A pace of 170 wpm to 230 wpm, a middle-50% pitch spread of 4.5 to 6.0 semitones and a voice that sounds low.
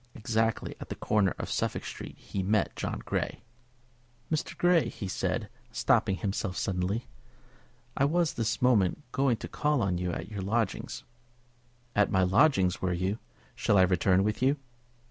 No: average, 160 wpm; average, 5.0 semitones; low, 105 Hz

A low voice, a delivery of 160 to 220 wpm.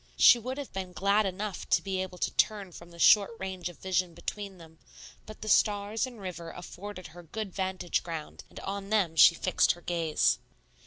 No: high, 190 Hz; average, 200 wpm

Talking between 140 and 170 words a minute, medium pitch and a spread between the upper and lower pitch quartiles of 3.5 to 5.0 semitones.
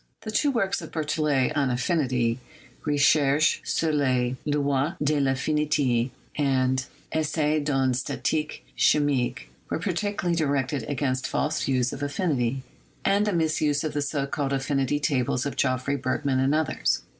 No: average, 150 wpm; medium, 145 Hz; average, 2.8 semitones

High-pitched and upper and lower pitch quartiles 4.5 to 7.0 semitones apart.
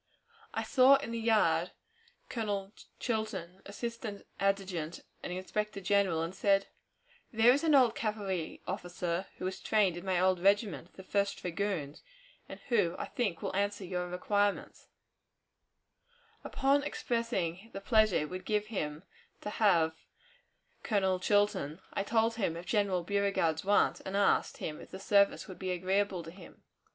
No: high, 195 Hz; average, 3.0 semitones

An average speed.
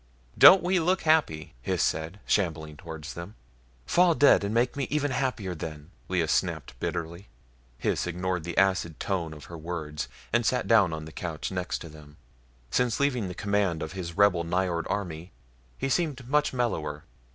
Yes: average, 170 wpm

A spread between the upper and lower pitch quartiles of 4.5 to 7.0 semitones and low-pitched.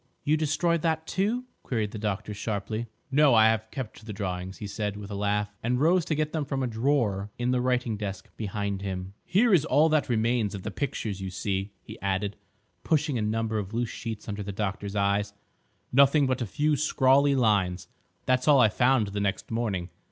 Yes: average, 5.3 semitones; low, 110 Hz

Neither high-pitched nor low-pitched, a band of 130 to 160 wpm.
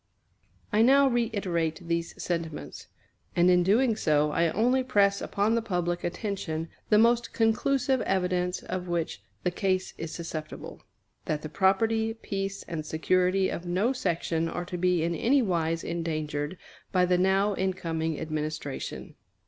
Yes: medium, 180 Hz; average, 140 wpm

